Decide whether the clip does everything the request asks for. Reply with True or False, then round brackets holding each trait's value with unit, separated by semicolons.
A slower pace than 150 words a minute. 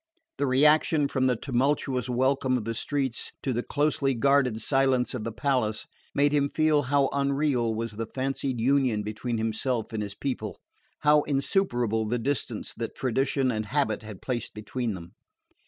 False (165 wpm)